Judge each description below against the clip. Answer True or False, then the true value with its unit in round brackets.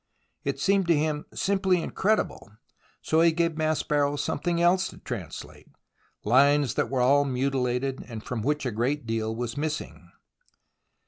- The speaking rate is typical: True (150 wpm)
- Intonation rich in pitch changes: False (4.7 semitones)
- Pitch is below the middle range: False (145 Hz)